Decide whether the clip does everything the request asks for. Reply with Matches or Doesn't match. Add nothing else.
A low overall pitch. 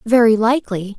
Doesn't match